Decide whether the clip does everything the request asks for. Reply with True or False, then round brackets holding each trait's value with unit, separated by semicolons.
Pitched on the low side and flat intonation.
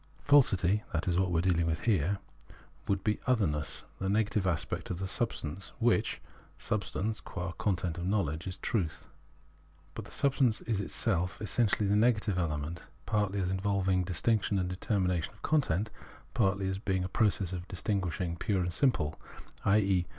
False (95 Hz; 3.1 semitones)